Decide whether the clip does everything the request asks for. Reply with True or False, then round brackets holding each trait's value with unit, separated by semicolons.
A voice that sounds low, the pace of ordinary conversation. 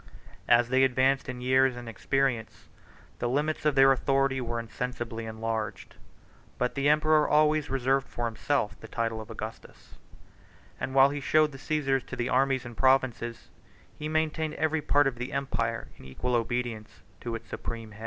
True (130 Hz; 170 wpm)